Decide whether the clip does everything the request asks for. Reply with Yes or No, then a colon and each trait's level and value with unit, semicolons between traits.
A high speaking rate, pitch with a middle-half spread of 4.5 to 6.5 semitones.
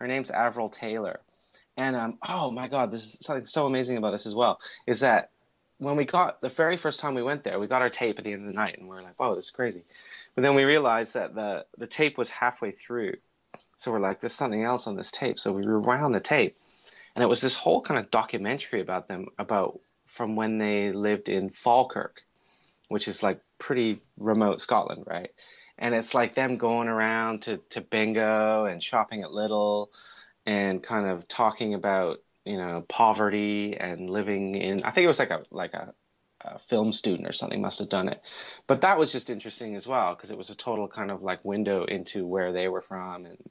No: fast, 225 wpm; average, 3.2 semitones